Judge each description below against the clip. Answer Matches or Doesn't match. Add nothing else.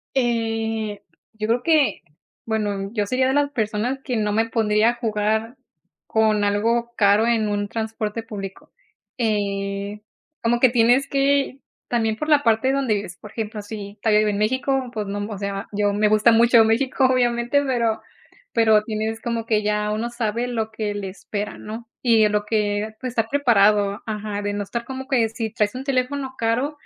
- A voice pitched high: Matches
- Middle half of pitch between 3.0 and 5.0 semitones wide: Doesn't match